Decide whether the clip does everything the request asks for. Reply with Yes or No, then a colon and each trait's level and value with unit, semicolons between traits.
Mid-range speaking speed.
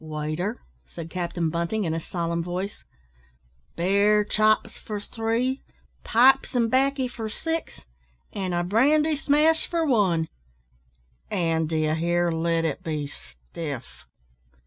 No: slow, 125 wpm